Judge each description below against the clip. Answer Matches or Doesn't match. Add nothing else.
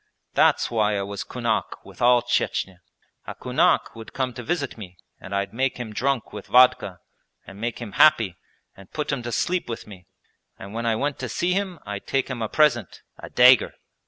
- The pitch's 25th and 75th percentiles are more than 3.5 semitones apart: Matches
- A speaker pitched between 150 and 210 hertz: Doesn't match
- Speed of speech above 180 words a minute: Matches